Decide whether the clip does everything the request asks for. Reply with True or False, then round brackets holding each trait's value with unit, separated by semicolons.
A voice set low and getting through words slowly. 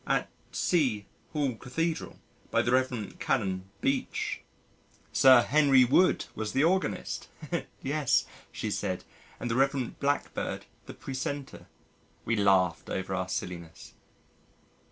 True (130 Hz; 115 wpm)